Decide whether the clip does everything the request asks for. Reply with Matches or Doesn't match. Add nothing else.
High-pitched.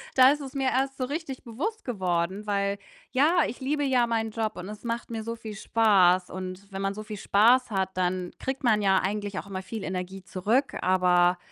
Matches